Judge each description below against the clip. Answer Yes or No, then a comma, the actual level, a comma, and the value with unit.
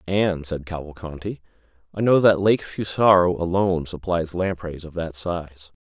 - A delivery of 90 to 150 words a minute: Yes, average, 145 wpm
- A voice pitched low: Yes, very low, 90 Hz